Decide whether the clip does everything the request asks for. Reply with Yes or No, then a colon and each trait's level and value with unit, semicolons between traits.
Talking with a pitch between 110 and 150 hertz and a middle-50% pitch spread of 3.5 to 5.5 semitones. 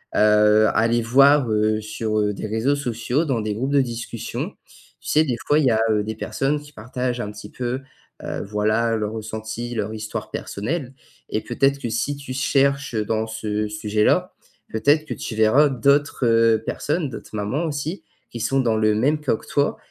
Yes: low, 115 Hz; average, 4.2 semitones